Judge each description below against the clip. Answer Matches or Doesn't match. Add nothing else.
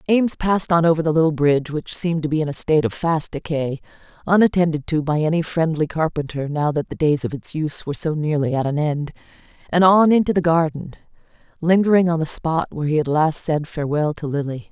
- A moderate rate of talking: Doesn't match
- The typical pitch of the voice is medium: Matches